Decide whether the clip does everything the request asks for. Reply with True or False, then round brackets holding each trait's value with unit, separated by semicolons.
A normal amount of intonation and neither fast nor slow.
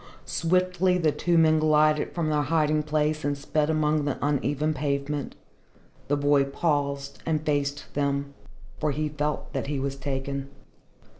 False (1.6 semitones; 150 wpm)